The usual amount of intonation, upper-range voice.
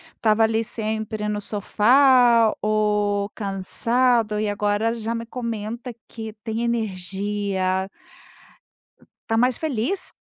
No: narrow, 2.1 semitones; high, 220 Hz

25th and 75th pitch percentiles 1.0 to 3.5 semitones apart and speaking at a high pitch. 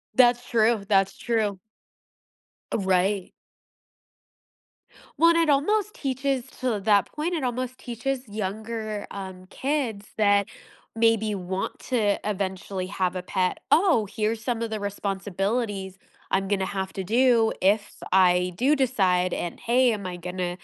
No: average, 4.3 semitones; high, 210 Hz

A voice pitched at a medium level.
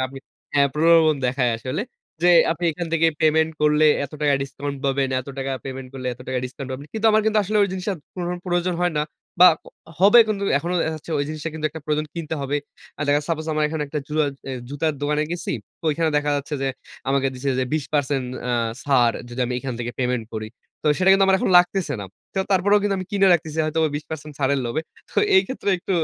Yes: medium, 150 Hz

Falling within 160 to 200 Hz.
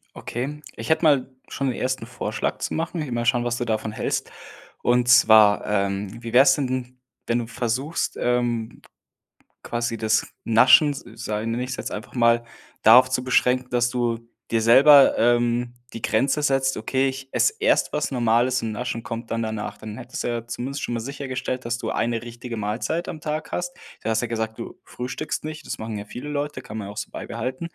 No: low, 120 Hz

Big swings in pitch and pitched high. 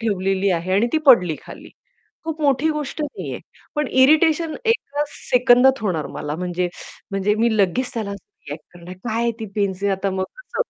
Yes: wide, 7.0 semitones; high, 220 Hz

